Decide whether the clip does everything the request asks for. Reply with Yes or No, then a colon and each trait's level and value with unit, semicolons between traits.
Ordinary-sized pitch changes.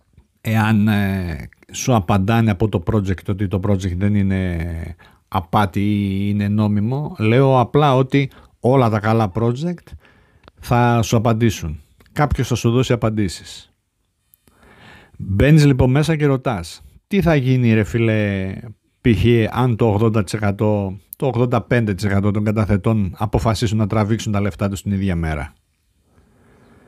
Yes: average, 3.4 semitones